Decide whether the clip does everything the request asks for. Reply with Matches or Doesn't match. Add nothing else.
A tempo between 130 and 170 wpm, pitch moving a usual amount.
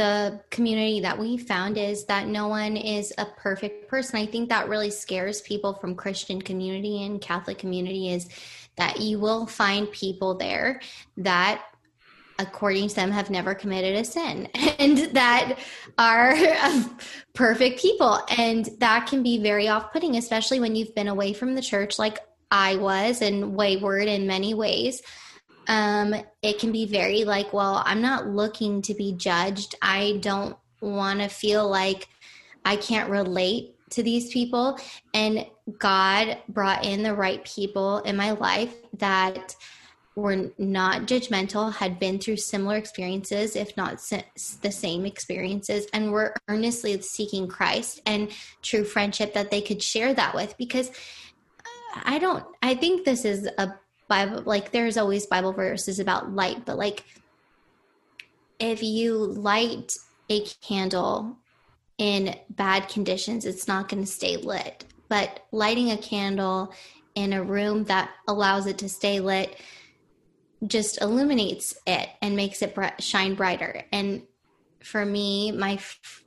Doesn't match